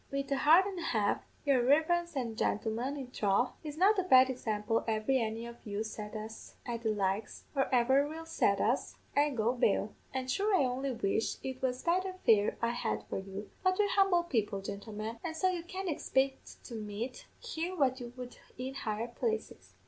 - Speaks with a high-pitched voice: Yes, very high, 255 Hz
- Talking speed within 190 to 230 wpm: Yes, average, 200 wpm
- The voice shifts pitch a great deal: Yes, wide, 6.2 semitones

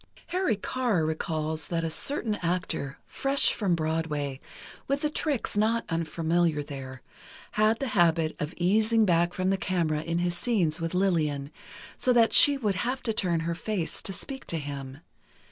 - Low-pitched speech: No, medium, 175 Hz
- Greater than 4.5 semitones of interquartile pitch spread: Yes, wide, 5.5 semitones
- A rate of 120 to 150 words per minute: No, average, 165 wpm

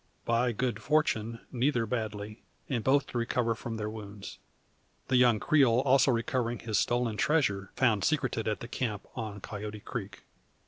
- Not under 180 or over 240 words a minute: No, average, 155 wpm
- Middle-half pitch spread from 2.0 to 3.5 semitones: Yes, average, 2.9 semitones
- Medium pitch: No, low, 115 Hz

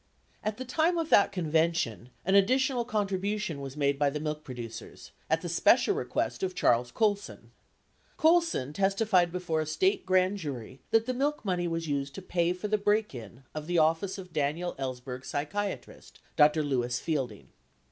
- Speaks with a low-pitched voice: No, medium, 175 Hz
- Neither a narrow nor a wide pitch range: No, wide, 6.4 semitones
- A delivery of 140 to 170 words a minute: No, average, 180 wpm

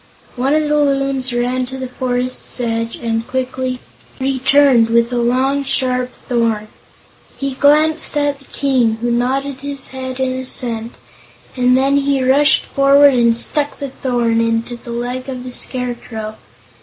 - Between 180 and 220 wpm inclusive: No, average, 155 wpm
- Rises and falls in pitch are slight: Yes, narrow, 2.3 semitones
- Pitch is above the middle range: Yes, very high, 255 Hz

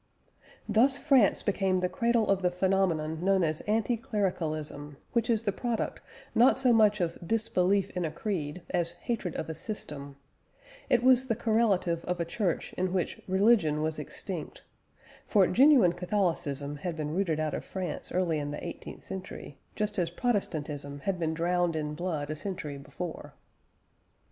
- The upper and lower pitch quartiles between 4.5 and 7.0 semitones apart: Yes, average, 4.9 semitones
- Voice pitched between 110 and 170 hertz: No, medium, 180 Hz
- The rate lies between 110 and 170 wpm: Yes, average, 165 wpm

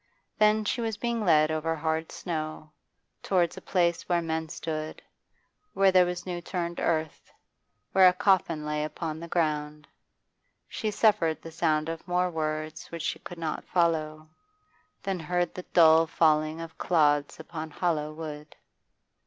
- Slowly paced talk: No, average, 155 wpm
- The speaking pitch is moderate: Yes, medium, 165 Hz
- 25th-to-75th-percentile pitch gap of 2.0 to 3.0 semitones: Yes, narrow, 2.4 semitones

